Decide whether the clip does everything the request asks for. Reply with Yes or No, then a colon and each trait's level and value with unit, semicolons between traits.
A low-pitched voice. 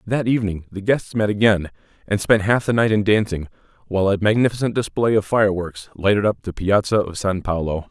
Yes: low, 100 Hz